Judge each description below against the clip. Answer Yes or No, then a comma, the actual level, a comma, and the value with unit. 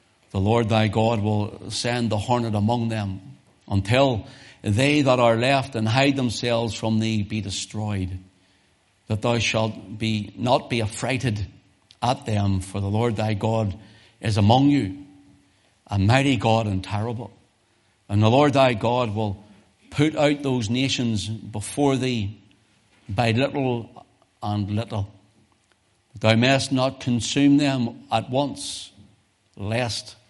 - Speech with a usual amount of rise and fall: Yes, average, 3.2 semitones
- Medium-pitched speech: No, low, 110 Hz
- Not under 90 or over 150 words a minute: Yes, slow, 135 wpm